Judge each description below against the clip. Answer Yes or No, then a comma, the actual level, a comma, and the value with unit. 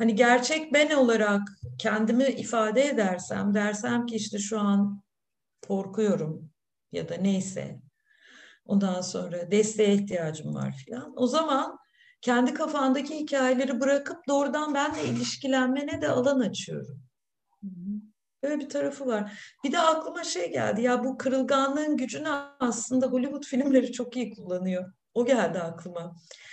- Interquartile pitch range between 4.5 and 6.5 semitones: Yes, wide, 5.6 semitones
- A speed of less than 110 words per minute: No, average, 125 wpm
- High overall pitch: Yes, high, 245 Hz